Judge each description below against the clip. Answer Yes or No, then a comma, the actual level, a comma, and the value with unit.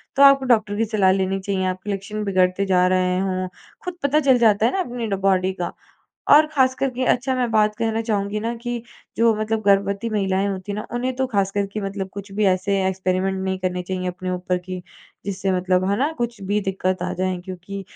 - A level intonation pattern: No, average, 3.3 semitones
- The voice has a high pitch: Yes, high, 200 Hz